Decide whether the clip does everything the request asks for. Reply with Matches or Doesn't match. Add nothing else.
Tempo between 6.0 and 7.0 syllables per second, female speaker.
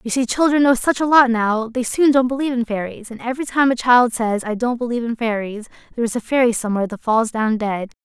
Matches